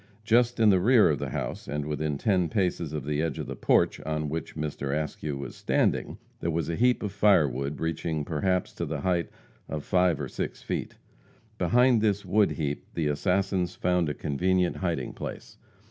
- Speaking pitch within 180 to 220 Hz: No, very low, 85 Hz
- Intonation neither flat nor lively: Yes, average, 4.4 semitones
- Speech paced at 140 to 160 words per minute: No, average, 190 wpm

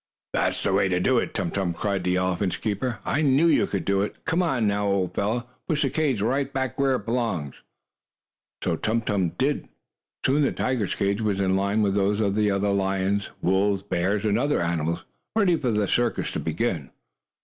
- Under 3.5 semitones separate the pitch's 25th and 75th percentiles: No, average, 4.4 semitones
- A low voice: Yes, low, 100 Hz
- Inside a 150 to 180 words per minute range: No, average, 200 wpm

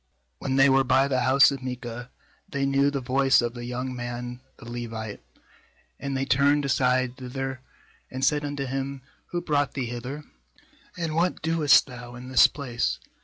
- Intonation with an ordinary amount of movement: No, narrow, 2.1 semitones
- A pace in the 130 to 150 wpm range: No, average, 170 wpm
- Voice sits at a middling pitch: No, low, 130 Hz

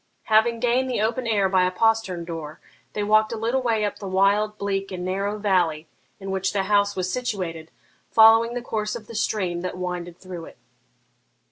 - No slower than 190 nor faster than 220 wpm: Yes, average, 195 wpm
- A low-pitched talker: No, high, 200 Hz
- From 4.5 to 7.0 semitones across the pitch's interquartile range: No, average, 3.4 semitones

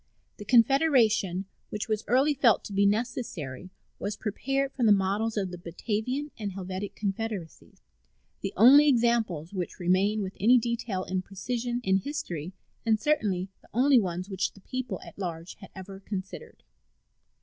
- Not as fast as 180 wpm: Yes, average, 155 wpm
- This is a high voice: Yes, high, 205 Hz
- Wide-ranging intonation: No, average, 4.2 semitones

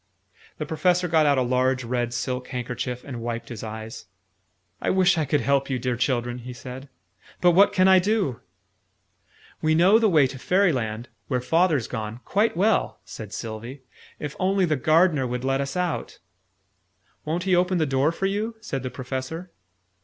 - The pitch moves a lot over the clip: Yes, wide, 6.2 semitones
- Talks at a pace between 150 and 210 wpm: Yes, average, 175 wpm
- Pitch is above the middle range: No, medium, 140 Hz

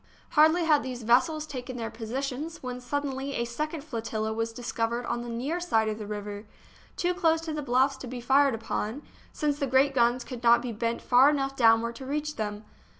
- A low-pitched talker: No, very high, 250 Hz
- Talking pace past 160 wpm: Yes, fast, 205 wpm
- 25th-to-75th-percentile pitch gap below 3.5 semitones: No, average, 3.8 semitones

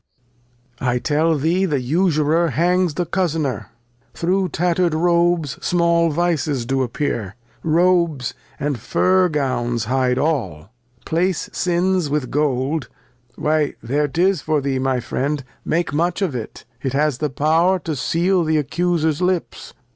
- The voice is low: No, medium, 155 Hz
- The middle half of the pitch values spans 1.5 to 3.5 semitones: No, average, 4.2 semitones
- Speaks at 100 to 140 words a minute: Yes, slow, 135 wpm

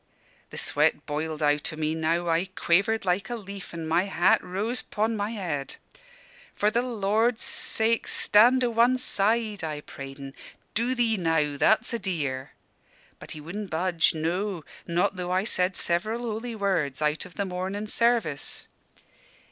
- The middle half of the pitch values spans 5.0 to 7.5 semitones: Yes, average, 5.3 semitones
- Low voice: No, high, 190 Hz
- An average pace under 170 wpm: Yes, average, 160 wpm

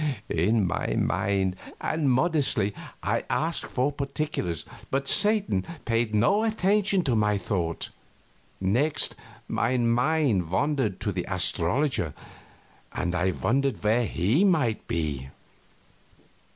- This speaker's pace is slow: Yes, slow, 110 wpm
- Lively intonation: Yes, wide, 7.9 semitones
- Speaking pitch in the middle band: No, low, 115 Hz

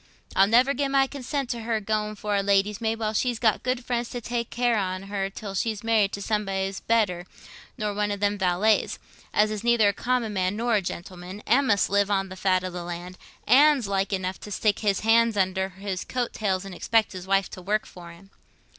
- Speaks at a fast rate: Yes, fast, 225 wpm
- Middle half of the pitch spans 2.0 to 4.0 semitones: Yes, average, 2.9 semitones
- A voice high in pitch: Yes, high, 205 Hz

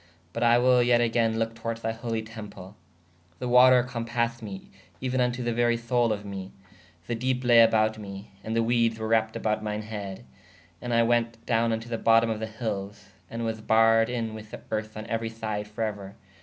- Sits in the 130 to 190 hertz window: No, low, 115 Hz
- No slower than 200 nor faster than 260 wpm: Yes, fast, 205 wpm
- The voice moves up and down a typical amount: No, narrow, 1.5 semitones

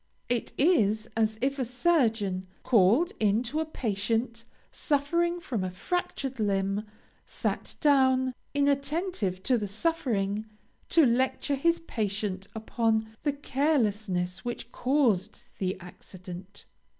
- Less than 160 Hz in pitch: No, high, 230 Hz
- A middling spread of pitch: No, wide, 5.7 semitones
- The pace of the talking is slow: Yes, slow, 115 wpm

